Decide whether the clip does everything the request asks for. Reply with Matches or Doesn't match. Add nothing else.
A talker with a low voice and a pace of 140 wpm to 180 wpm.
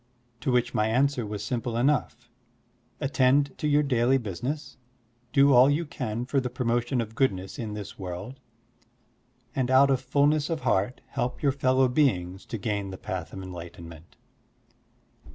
Matches